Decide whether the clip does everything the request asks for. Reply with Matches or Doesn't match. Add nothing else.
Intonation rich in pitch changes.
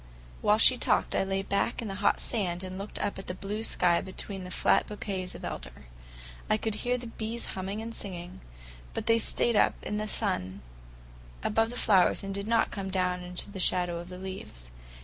Doesn't match